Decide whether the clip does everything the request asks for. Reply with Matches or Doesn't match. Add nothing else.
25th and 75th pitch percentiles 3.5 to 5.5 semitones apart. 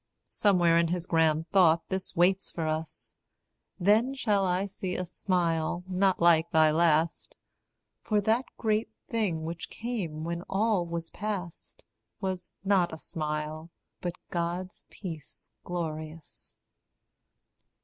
Doesn't match